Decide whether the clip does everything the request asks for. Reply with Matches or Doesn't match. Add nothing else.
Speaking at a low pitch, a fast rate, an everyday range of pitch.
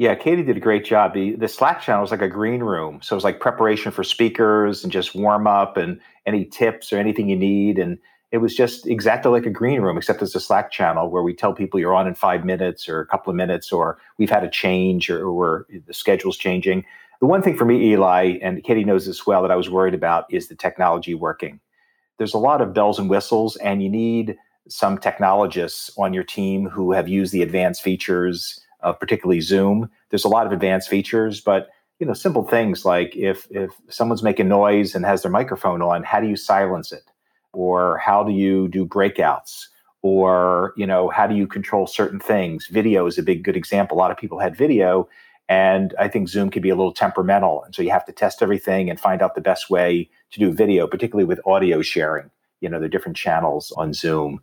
Doesn't match